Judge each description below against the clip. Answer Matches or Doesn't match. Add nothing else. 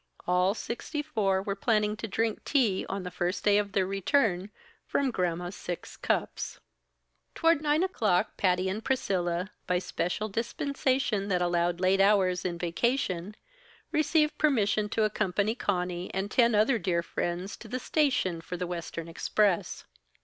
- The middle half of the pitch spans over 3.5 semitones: Matches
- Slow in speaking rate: Doesn't match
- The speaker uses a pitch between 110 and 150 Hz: Doesn't match